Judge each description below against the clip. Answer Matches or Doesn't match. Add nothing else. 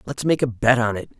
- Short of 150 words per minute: Doesn't match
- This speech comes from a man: Matches